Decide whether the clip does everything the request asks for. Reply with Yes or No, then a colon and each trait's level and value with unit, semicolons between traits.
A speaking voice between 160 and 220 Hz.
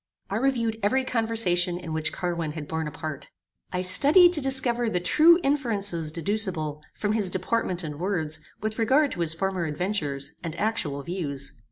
Yes: medium, 185 Hz